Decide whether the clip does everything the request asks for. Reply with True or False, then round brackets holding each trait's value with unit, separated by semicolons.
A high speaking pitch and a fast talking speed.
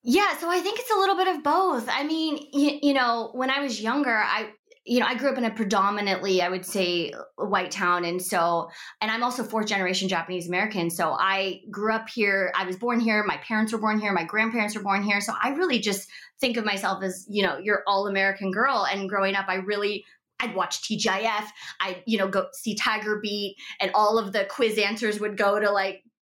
True (210 Hz; 225 wpm)